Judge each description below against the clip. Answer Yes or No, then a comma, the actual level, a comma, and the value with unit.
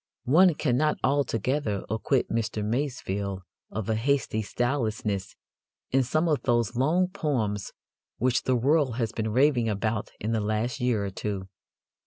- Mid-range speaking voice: No, low, 120 Hz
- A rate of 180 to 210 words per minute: No, average, 145 wpm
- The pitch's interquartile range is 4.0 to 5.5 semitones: Yes, average, 4.4 semitones